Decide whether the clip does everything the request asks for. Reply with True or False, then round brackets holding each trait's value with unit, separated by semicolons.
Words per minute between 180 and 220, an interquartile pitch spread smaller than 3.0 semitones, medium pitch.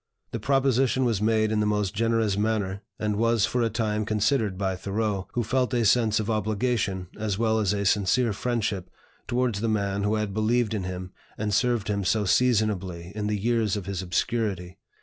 False (190 wpm; 2.5 semitones; 105 Hz)